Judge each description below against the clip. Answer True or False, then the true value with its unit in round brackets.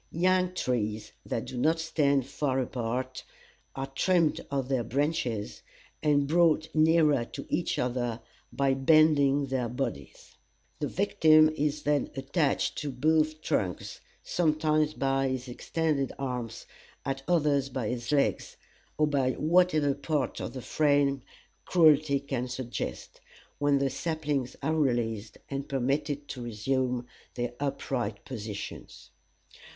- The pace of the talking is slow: True (125 wpm)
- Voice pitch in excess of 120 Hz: True (140 Hz)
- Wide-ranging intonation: False (3.4 semitones)